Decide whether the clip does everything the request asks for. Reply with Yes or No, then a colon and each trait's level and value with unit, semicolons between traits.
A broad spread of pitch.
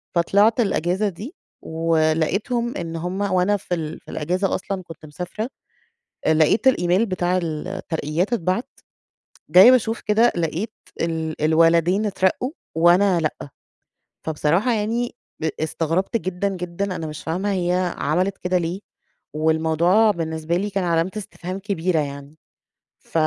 No: average, 3.7 semitones